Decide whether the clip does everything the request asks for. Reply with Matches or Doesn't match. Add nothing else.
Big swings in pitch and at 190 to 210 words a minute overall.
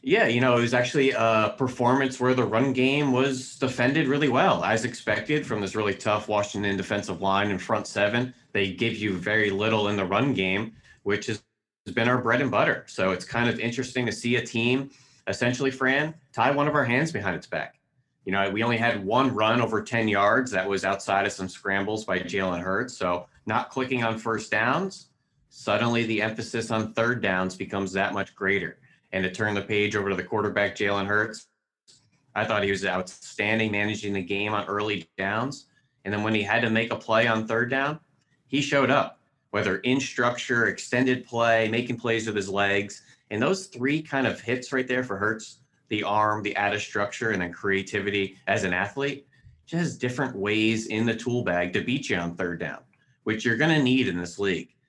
Doesn't match